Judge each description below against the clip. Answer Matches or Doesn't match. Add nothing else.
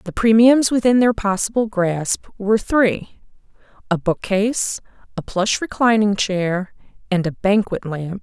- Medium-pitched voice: Doesn't match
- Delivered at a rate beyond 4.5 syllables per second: Doesn't match